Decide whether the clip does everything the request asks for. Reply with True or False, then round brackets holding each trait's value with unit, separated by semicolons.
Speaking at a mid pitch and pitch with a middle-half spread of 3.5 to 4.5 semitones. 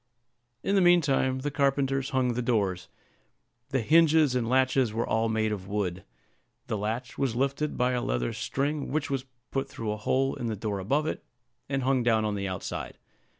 False (125 Hz; 4.1 semitones)